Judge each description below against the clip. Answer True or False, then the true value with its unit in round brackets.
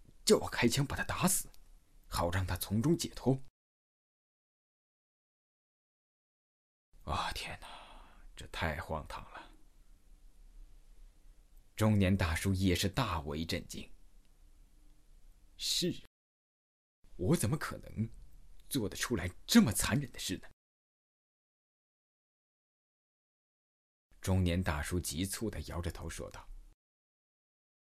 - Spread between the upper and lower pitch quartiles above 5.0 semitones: False (4.6 semitones)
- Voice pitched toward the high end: False (90 Hz)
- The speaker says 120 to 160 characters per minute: True (135 characters per minute)